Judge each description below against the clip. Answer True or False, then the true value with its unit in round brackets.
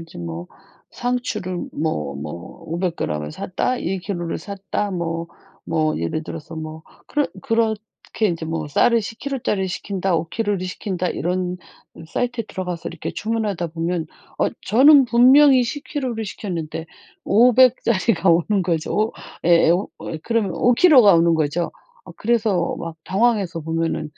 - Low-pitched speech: False (185 Hz)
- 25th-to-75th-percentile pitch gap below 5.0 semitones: False (5.5 semitones)